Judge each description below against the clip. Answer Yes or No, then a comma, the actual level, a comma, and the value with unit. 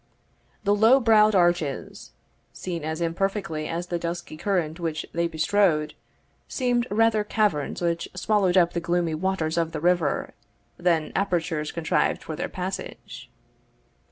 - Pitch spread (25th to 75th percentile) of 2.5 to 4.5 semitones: Yes, average, 3.5 semitones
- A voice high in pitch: No, medium, 175 Hz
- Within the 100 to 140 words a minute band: Yes, slow, 135 wpm